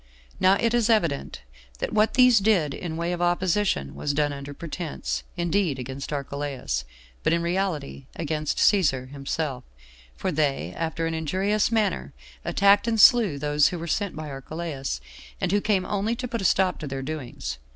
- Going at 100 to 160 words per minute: No, average, 170 wpm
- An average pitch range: No, wide, 5.9 semitones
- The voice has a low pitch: No, medium, 165 Hz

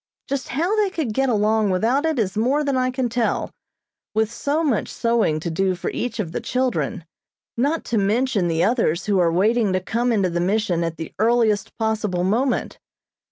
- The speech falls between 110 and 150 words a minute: No, average, 195 wpm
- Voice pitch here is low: No, high, 220 Hz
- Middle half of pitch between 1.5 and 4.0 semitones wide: No, average, 5.1 semitones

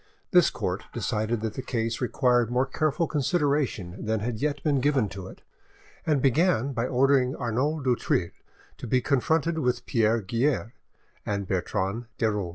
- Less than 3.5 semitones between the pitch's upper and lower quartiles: No, average, 4.3 semitones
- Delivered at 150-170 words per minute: Yes, average, 165 wpm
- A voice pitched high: No, low, 125 Hz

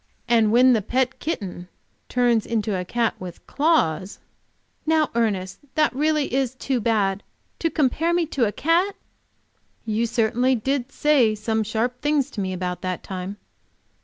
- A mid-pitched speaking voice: No, high, 235 Hz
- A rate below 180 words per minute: Yes, average, 155 wpm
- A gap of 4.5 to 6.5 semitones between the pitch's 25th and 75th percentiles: Yes, average, 5.3 semitones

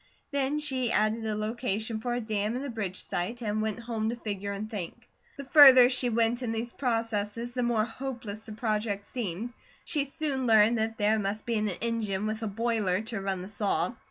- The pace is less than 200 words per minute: No, fast, 205 wpm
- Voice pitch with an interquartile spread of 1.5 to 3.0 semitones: Yes, narrow, 2.4 semitones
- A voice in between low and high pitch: No, high, 225 Hz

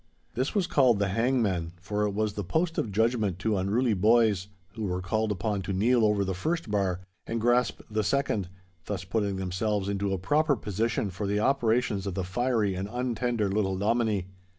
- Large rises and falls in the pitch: No, average, 3.4 semitones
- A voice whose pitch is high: No, low, 105 Hz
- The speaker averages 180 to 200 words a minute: Yes, average, 190 wpm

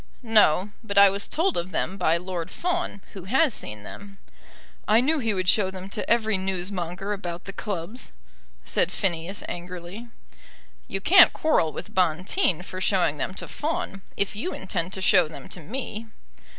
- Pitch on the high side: Yes, high, 195 Hz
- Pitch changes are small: No, average, 3.6 semitones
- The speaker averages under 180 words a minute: Yes, average, 170 wpm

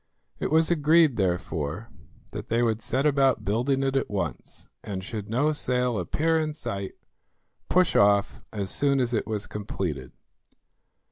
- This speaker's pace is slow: No, average, 150 wpm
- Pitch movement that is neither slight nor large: No, wide, 5.9 semitones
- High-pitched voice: No, low, 115 Hz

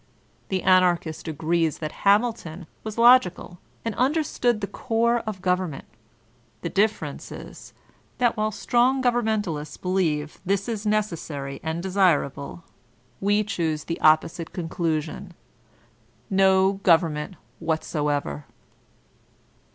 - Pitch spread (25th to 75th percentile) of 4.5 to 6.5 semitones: Yes, average, 4.9 semitones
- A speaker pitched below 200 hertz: Yes, medium, 185 Hz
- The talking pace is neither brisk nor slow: No, slow, 105 wpm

